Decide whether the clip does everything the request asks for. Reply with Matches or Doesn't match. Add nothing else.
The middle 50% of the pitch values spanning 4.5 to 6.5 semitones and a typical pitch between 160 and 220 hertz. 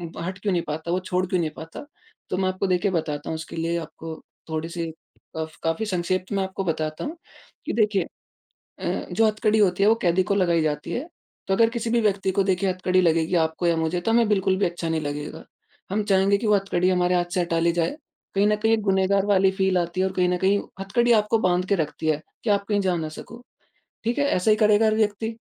Doesn't match